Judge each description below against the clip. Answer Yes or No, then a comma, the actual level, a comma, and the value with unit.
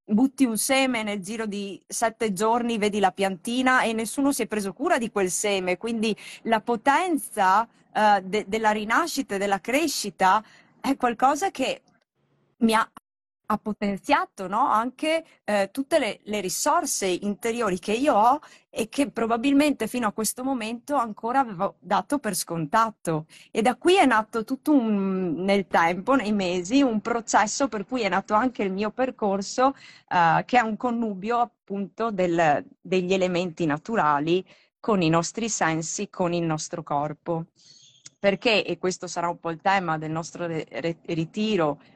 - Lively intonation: No, average, 4.6 semitones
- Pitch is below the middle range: No, high, 215 Hz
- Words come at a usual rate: Yes, average, 155 wpm